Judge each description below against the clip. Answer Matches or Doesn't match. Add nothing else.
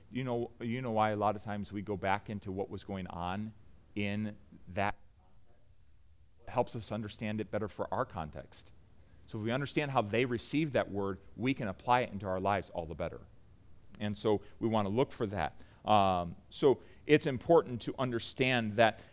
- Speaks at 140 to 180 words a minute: Doesn't match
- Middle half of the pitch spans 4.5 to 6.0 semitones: Doesn't match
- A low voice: Matches